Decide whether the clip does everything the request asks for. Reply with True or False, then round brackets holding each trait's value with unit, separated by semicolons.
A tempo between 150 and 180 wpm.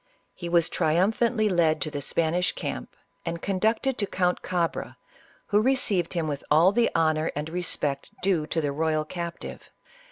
True (165 wpm)